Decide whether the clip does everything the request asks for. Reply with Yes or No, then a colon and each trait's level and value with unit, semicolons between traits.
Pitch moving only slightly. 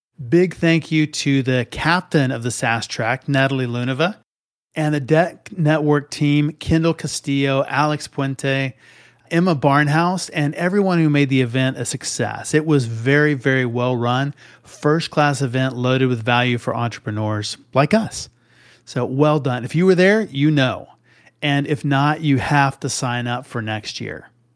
No: average, 3.3 semitones